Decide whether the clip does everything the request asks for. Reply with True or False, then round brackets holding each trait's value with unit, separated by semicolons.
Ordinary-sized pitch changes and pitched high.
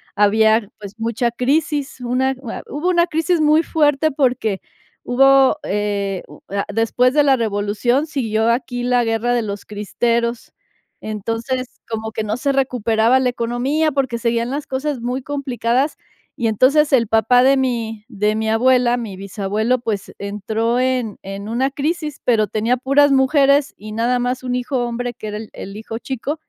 True (3.4 semitones; 245 Hz)